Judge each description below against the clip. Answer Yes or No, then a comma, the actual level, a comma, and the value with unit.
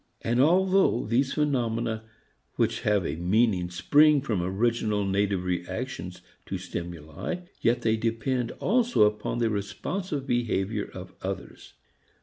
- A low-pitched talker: Yes, low, 110 Hz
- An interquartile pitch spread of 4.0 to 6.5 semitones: Yes, average, 5.2 semitones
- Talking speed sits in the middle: No, slow, 125 wpm